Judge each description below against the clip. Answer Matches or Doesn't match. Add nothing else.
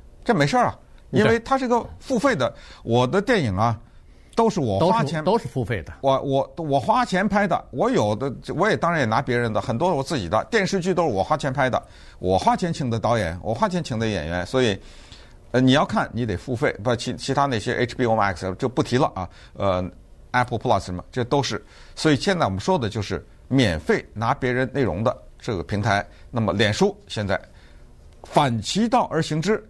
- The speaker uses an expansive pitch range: Matches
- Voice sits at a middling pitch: Doesn't match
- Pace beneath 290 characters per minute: Doesn't match